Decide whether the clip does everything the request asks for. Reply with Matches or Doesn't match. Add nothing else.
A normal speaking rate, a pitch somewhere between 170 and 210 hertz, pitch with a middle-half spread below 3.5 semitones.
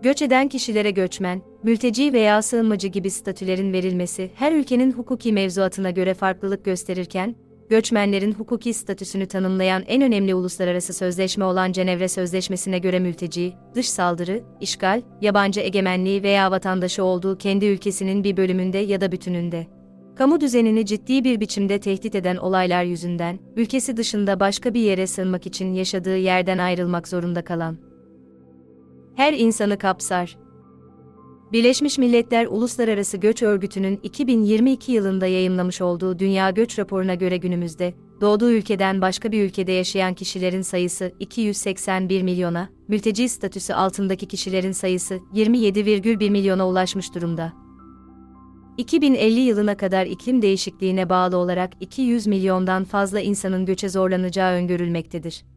Matches